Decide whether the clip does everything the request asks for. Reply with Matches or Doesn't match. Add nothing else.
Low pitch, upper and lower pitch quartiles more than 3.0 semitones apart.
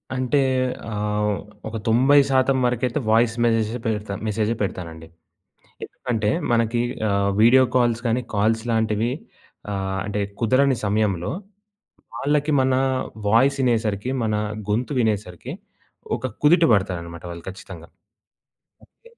Matches